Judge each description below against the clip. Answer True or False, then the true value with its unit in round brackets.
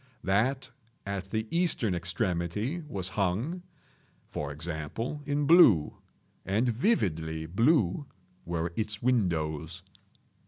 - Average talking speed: False (90 wpm)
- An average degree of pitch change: False (6.8 semitones)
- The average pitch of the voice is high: False (100 Hz)